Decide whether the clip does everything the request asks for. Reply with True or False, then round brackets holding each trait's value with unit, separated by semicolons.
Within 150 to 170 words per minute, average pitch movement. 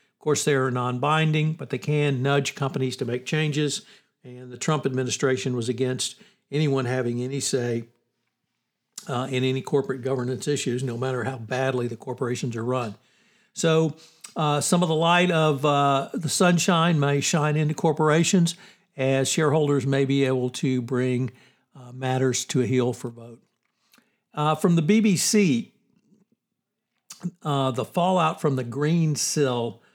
True (155 wpm; 3.9 semitones)